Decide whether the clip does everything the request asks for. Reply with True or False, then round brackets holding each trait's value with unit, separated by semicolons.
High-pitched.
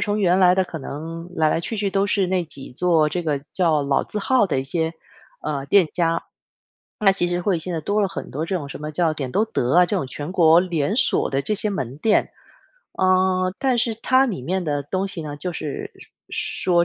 False (175 Hz)